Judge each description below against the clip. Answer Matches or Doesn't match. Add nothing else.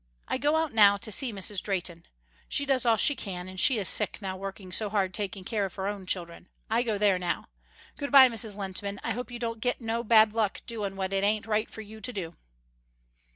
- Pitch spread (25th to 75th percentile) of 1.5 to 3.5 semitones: Matches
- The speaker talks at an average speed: Doesn't match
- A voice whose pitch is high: Matches